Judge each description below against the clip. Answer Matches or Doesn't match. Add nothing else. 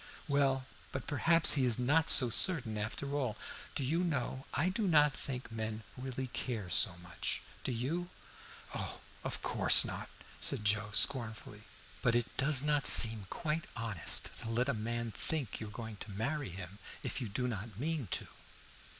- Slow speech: Doesn't match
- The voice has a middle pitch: Doesn't match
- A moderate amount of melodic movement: Matches